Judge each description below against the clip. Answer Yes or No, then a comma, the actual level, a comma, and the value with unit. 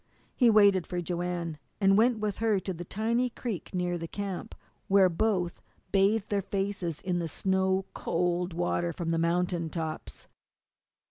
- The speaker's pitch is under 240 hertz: Yes, medium, 185 Hz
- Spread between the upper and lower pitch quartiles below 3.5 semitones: Yes, average, 2.7 semitones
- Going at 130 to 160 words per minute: Yes, average, 155 wpm